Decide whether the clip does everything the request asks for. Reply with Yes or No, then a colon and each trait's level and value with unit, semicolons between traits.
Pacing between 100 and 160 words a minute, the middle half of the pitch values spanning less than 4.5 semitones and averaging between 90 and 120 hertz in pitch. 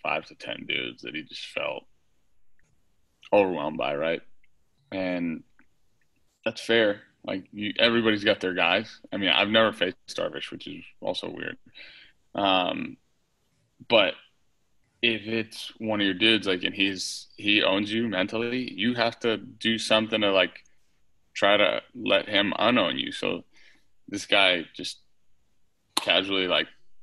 Yes: average, 140 wpm; narrow, 2.5 semitones; low, 110 Hz